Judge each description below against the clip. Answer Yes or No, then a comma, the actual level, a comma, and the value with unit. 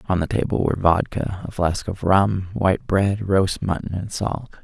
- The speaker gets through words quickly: No, average, 195 wpm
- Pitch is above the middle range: No, very low, 95 Hz